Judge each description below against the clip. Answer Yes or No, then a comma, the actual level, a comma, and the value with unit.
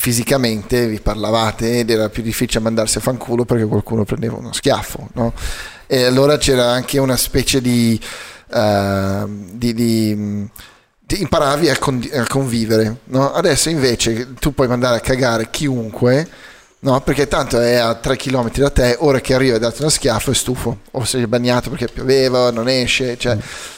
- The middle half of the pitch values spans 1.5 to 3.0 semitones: Yes, narrow, 2.6 semitones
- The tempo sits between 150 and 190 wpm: Yes, fast, 170 wpm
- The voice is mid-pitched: No, low, 120 Hz